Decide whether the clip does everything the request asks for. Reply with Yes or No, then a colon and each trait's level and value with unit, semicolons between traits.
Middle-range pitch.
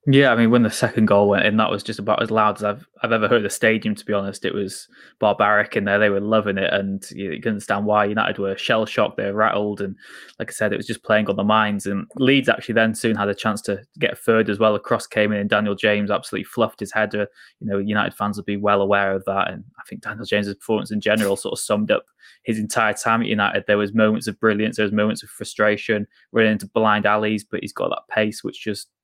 No: low, 105 Hz